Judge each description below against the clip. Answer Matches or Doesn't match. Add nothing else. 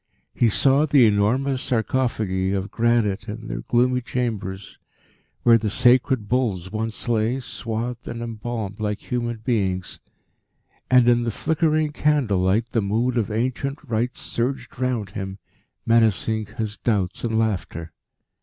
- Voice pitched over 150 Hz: Doesn't match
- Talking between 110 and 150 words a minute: Matches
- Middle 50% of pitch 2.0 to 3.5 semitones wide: Matches